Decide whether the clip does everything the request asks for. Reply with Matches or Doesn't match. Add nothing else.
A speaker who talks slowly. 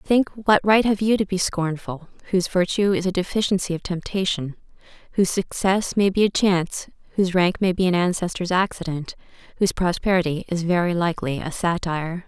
Doesn't match